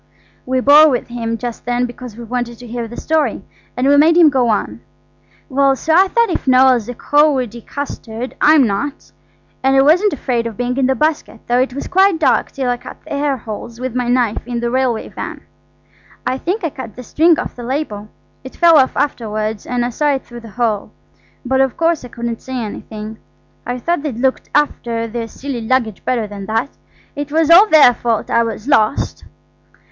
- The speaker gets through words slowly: No, fast, 205 wpm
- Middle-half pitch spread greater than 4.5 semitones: No, average, 3.6 semitones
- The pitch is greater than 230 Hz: Yes, very high, 250 Hz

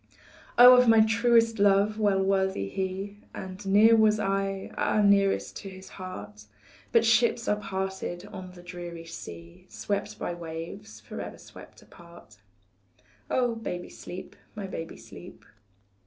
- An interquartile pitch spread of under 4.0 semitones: Yes, average, 3.5 semitones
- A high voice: Yes, high, 195 Hz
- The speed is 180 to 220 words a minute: No, average, 140 wpm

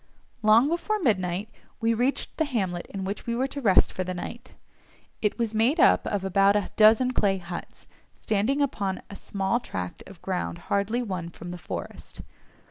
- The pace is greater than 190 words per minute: No, average, 180 wpm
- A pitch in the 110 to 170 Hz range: No, high, 205 Hz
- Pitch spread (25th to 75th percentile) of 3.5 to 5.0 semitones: Yes, average, 4.2 semitones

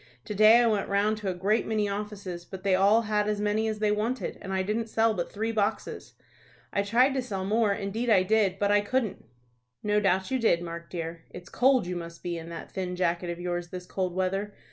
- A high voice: Yes, high, 200 Hz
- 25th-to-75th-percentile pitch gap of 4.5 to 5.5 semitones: No, average, 3.0 semitones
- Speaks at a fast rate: Yes, fast, 230 wpm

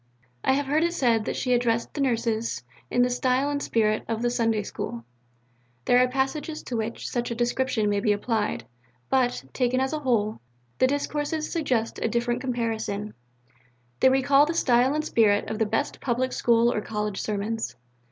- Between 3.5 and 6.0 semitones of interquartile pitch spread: No, average, 3.1 semitones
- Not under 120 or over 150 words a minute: No, average, 180 wpm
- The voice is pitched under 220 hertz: No, high, 240 Hz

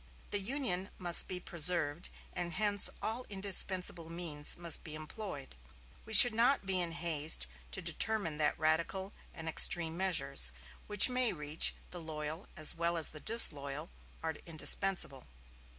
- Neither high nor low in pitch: Yes, medium, 170 Hz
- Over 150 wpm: No, average, 145 wpm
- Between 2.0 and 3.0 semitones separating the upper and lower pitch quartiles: No, average, 3.8 semitones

